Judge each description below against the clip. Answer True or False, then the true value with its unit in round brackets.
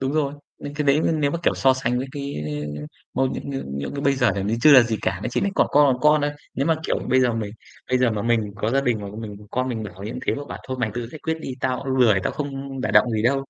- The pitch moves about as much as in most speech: True (3.3 semitones)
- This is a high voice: False (130 Hz)